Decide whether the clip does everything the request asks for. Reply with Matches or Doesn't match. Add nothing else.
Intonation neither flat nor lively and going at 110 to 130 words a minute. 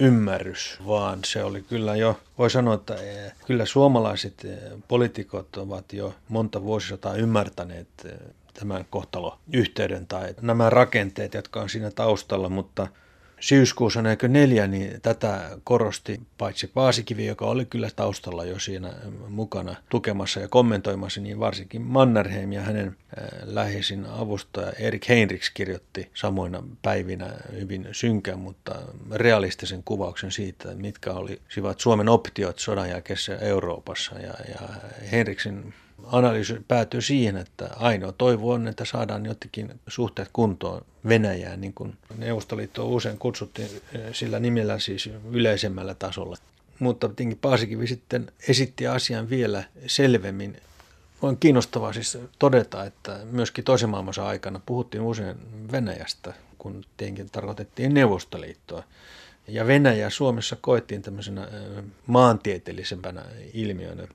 Matches